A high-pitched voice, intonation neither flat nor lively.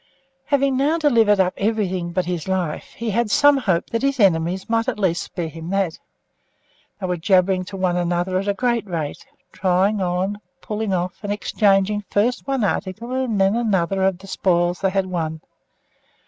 Yes: high, 195 Hz; average, 3.7 semitones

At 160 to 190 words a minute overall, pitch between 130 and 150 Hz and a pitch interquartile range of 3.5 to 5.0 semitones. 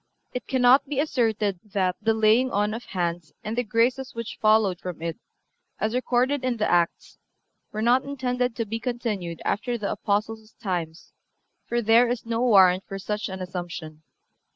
No: average, 170 wpm; high, 220 Hz; average, 4.4 semitones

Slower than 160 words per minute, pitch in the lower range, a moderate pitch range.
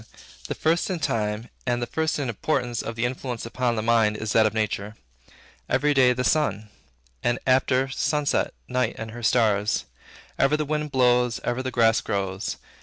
No: average, 180 wpm; low, 120 Hz; average, 3.2 semitones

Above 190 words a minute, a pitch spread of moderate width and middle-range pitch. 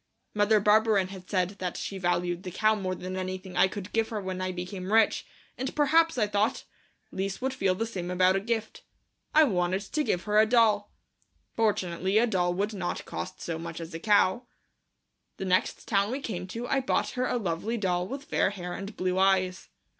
No: fast, 205 wpm; average, 3.2 semitones; high, 195 Hz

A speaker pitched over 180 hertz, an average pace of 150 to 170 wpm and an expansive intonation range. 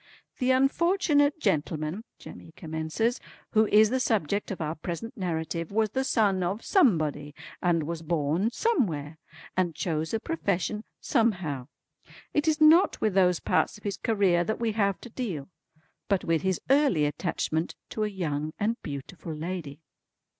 Yes: high, 190 Hz; average, 155 wpm; wide, 6.1 semitones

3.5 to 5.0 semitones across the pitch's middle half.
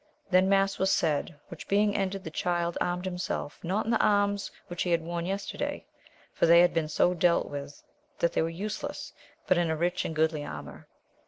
No: average, 2.9 semitones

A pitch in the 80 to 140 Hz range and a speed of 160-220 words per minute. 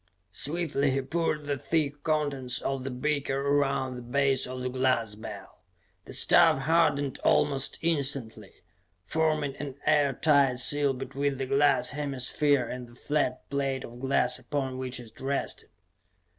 No: low, 135 Hz; average, 145 wpm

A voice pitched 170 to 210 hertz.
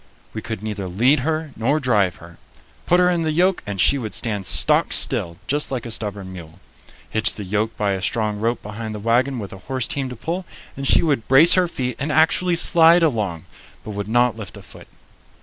No: low, 115 Hz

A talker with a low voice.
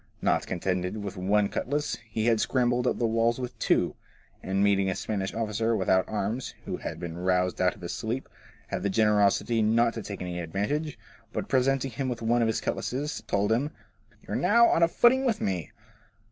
Yes: low, 110 Hz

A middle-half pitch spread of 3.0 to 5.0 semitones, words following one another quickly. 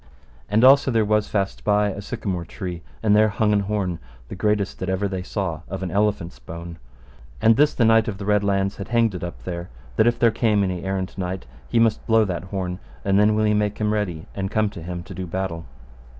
No: narrow, 2.6 semitones; fast, 230 wpm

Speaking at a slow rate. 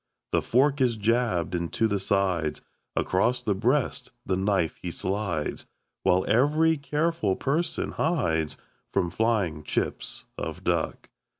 Yes: slow, 125 wpm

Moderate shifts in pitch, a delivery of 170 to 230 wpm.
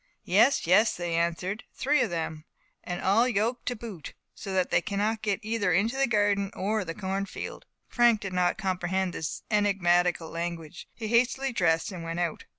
Yes: average, 4.0 semitones; average, 175 wpm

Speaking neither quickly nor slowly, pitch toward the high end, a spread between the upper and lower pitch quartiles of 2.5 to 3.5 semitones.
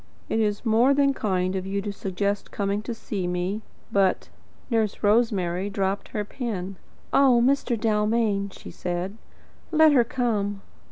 Yes: average, 155 wpm; high, 205 Hz; average, 3.2 semitones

